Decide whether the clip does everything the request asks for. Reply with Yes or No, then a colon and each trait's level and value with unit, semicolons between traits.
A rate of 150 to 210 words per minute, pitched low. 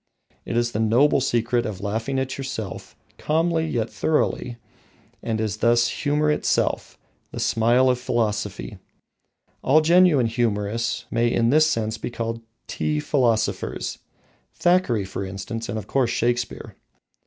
No: slow, 135 wpm; low, 120 Hz